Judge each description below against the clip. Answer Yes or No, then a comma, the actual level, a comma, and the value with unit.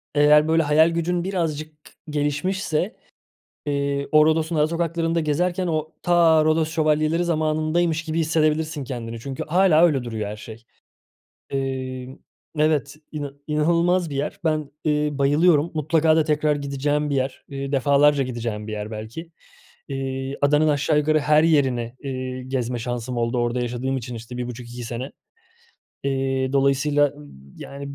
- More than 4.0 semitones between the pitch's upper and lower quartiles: No, average, 3.1 semitones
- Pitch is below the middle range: No, medium, 145 Hz